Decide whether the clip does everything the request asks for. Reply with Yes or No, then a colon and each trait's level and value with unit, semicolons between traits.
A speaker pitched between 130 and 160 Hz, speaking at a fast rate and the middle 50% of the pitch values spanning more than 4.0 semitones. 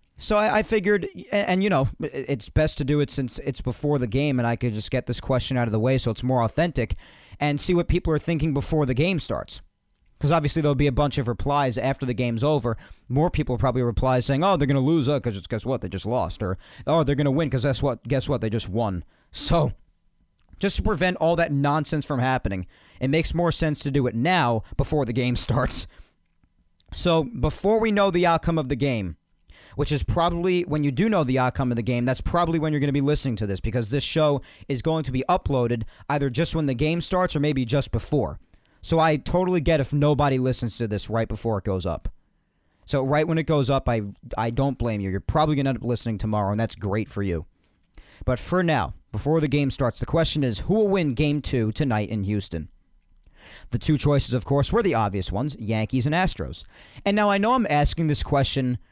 Yes: low, 135 Hz; fast, 235 wpm; wide, 5.4 semitones